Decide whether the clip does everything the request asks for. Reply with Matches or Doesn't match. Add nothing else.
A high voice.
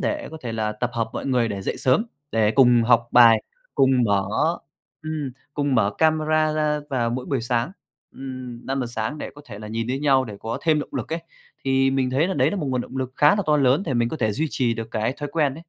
Doesn't match